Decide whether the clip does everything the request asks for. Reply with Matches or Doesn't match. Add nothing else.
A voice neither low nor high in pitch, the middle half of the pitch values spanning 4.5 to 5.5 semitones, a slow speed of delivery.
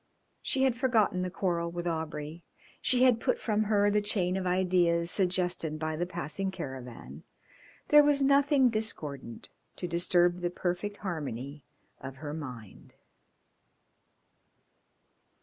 Matches